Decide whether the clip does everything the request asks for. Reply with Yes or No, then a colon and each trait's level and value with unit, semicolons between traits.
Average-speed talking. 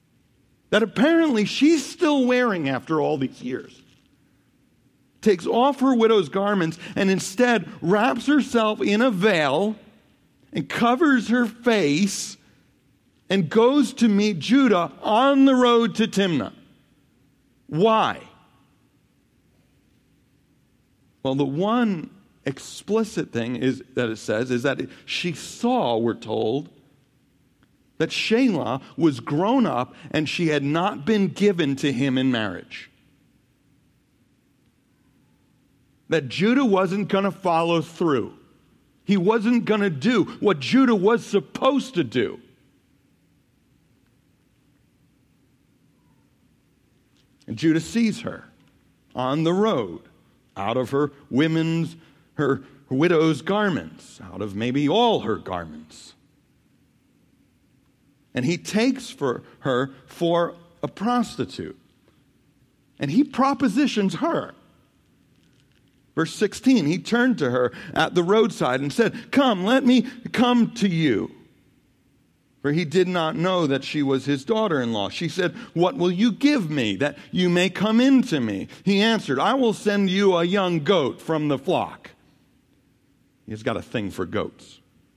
No: slow, 125 wpm